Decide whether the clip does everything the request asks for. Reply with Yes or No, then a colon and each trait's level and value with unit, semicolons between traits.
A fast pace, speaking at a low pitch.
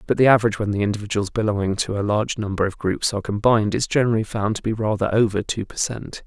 Yes: fast, 240 wpm; low, 105 Hz